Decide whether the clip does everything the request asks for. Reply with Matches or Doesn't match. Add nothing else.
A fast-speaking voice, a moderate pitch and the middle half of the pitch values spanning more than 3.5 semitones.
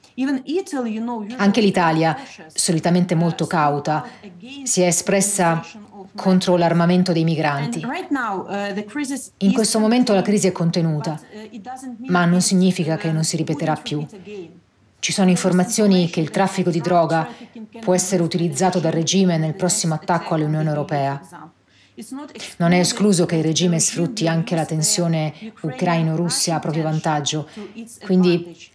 Doesn't match